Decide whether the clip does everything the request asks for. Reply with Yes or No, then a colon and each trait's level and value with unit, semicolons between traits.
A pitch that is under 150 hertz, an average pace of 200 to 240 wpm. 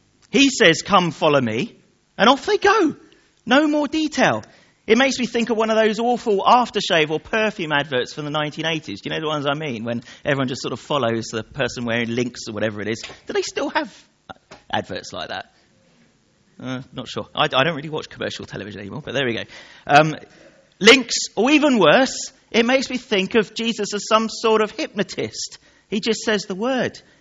No: high, 210 Hz; fast, 205 wpm